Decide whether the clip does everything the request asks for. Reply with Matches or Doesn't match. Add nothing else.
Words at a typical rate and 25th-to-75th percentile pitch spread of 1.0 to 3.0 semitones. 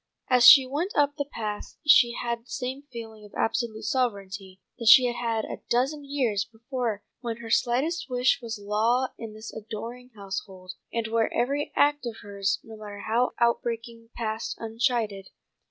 Matches